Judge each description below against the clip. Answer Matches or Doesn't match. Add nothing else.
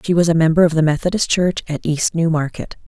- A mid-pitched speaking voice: Matches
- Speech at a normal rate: Doesn't match